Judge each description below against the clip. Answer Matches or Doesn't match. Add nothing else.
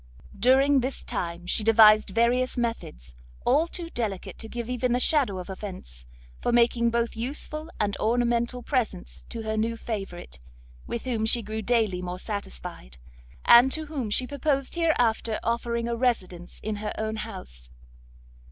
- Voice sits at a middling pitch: Doesn't match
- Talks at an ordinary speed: Matches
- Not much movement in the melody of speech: Doesn't match